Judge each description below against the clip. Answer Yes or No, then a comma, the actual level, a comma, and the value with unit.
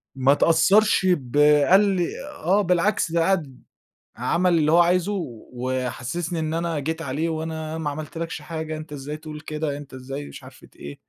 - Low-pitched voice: No, medium, 160 Hz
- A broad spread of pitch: No, average, 2.8 semitones